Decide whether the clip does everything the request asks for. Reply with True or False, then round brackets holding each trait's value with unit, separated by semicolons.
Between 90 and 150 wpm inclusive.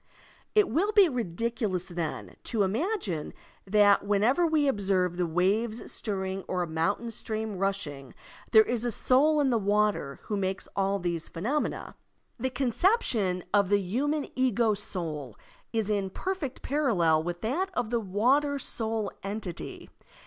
True (145 wpm)